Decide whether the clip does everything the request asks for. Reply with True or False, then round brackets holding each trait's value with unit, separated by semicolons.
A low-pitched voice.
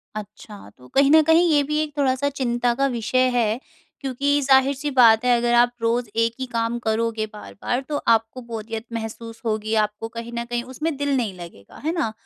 False (240 Hz)